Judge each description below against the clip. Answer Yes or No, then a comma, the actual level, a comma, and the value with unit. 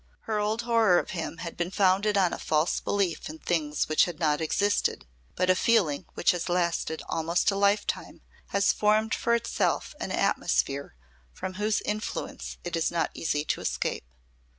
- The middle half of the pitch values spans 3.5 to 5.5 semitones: Yes, average, 4.1 semitones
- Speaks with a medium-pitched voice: Yes, medium, 180 Hz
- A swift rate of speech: No, average, 175 wpm